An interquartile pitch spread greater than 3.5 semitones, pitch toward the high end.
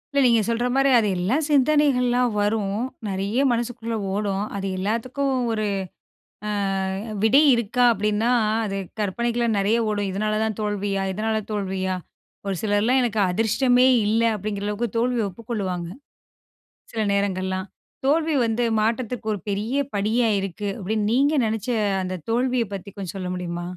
No: average, 3.2 semitones; high, 215 Hz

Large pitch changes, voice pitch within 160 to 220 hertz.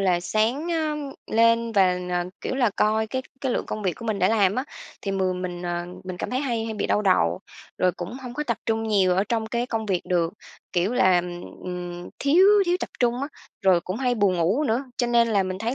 No: average, 4.7 semitones; high, 215 Hz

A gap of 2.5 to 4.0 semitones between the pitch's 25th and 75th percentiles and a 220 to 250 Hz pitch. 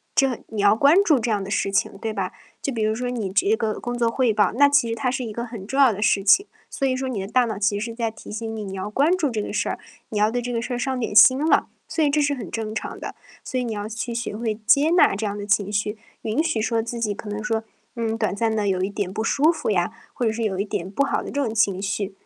Yes: average, 3.2 semitones; high, 225 Hz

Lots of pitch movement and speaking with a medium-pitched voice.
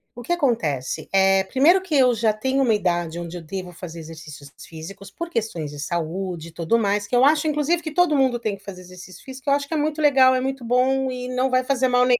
No: wide, 7.0 semitones; high, 230 Hz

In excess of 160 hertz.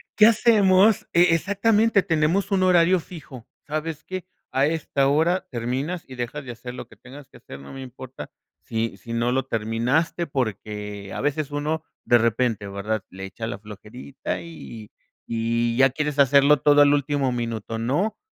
No: low, 135 Hz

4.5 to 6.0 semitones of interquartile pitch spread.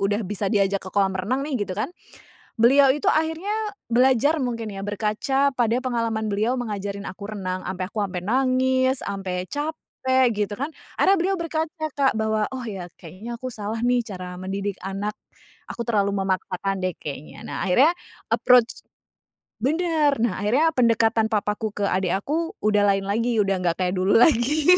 Yes: average, 4.9 semitones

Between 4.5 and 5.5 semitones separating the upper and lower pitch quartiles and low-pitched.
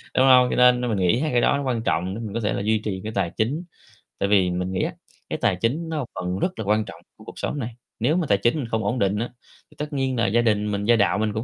No: average, 3.9 semitones; low, 110 Hz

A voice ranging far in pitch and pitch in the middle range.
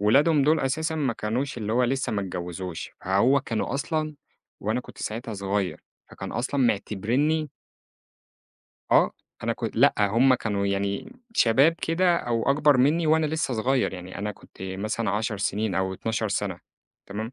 No: wide, 5.9 semitones; low, 115 Hz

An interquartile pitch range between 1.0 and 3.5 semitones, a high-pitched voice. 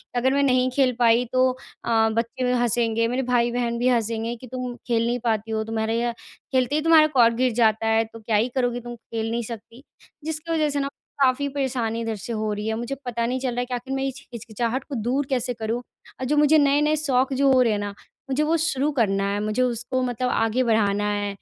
Yes: narrow, 2.5 semitones; high, 240 Hz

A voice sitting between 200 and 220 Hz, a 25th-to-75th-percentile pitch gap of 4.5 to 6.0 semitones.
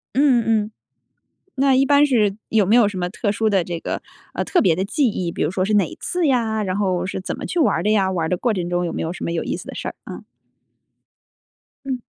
Yes: high, 205 Hz; average, 5.0 semitones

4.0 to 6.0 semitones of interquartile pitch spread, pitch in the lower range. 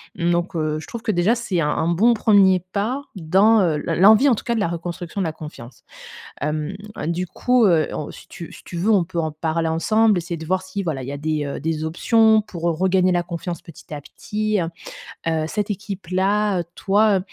No: average, 4.3 semitones; medium, 180 Hz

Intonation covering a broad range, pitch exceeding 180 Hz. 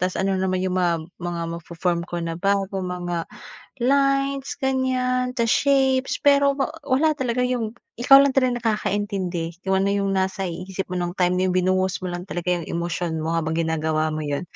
Yes: wide, 6.3 semitones; high, 190 Hz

